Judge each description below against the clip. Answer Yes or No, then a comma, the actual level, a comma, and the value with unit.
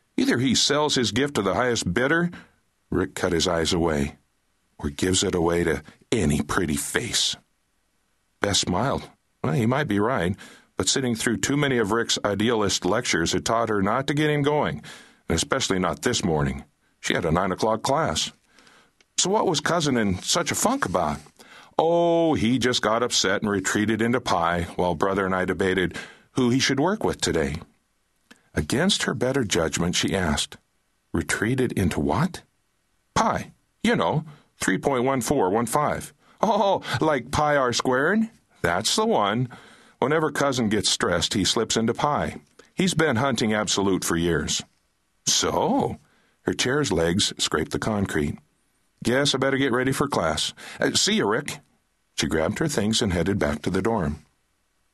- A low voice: Yes, low, 115 Hz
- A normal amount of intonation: No, wide, 6.6 semitones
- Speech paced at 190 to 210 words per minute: No, average, 160 wpm